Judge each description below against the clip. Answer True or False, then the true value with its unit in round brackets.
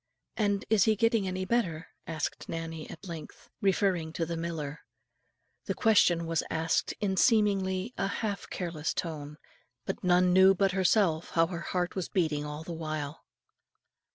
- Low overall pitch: False (175 Hz)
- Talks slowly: False (155 wpm)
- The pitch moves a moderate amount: True (3.2 semitones)